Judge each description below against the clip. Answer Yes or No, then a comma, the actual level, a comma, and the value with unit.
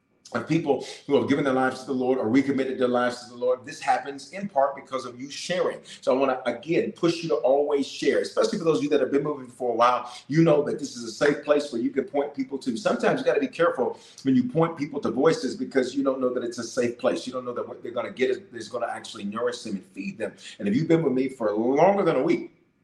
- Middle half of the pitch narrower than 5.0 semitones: Yes, average, 4.1 semitones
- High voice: No, low, 135 Hz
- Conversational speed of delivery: No, fast, 295 wpm